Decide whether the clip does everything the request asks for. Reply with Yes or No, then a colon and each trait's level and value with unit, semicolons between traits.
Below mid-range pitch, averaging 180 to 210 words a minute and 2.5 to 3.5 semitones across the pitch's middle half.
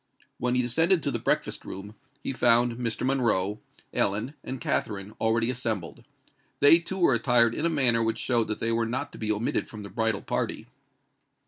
Yes: low, 115 Hz; average, 190 wpm; average, 2.8 semitones